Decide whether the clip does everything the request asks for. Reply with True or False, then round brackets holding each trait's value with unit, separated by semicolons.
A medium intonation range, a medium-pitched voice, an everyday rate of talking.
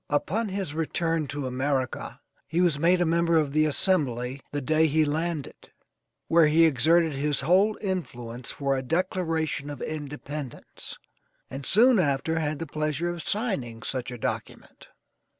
True (3.5 semitones; 155 Hz; 150 wpm)